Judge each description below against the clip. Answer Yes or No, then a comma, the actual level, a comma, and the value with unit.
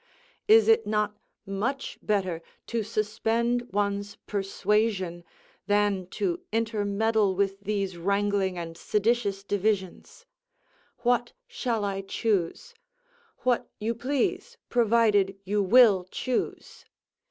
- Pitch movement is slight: No, average, 3.0 semitones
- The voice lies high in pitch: Yes, high, 210 Hz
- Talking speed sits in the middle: No, slow, 100 wpm